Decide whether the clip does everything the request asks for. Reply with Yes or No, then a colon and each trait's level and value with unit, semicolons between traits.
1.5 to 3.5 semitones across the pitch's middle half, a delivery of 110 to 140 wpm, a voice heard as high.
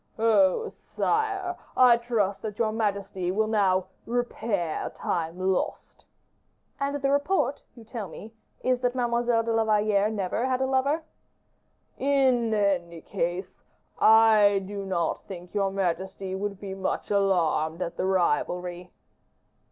No: average, 4.2 semitones; slow, 135 wpm; high, 205 Hz